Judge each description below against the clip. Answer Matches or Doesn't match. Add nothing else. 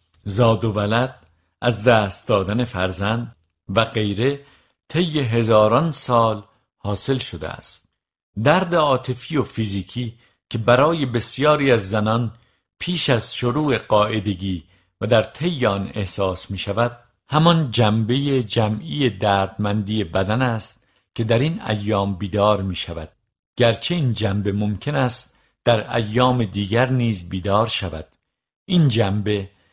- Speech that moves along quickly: Doesn't match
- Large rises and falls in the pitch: Doesn't match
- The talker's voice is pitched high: Doesn't match